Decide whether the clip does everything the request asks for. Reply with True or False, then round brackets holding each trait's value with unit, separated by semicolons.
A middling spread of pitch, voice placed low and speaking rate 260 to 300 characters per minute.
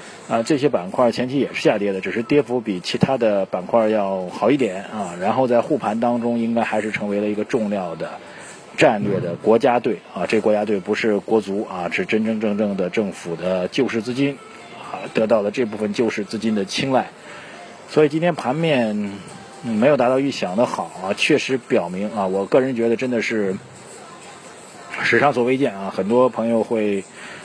True (3.1 semitones; 110 Hz; 285 characters per minute)